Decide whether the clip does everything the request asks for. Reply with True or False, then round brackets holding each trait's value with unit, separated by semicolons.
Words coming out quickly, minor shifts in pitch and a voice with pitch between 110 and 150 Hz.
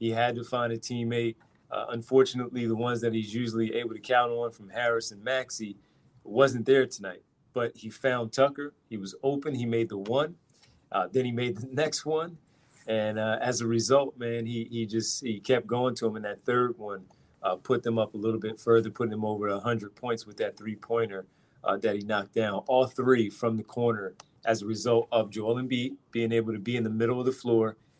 True (220 wpm; 2.2 semitones; 115 Hz)